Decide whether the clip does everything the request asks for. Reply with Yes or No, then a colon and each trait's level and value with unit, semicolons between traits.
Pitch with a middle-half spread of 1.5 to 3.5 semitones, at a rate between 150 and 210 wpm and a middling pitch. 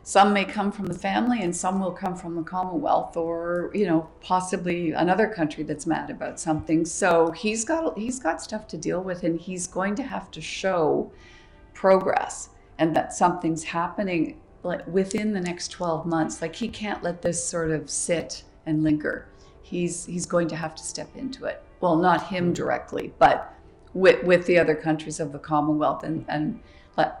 Yes: average, 3.0 semitones; average, 190 wpm; medium, 175 Hz